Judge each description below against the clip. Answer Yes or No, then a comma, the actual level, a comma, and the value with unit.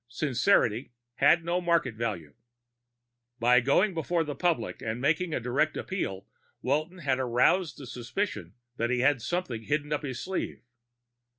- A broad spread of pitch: Yes, wide, 5.7 semitones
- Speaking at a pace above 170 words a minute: No, average, 150 wpm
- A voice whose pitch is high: No, medium, 140 Hz